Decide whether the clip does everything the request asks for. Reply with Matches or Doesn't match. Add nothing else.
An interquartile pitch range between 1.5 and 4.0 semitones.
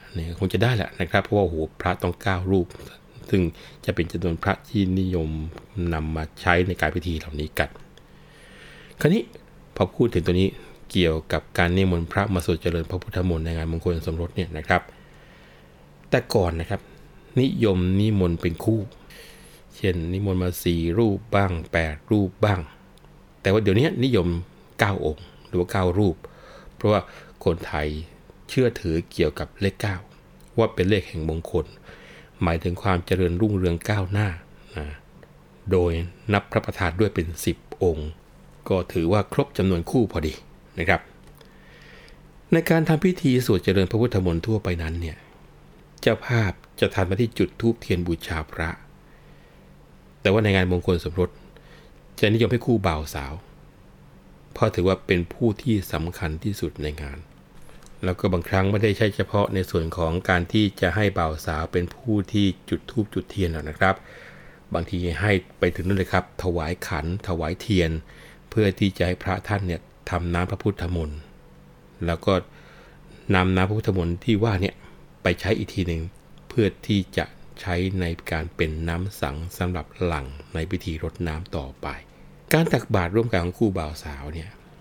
Matches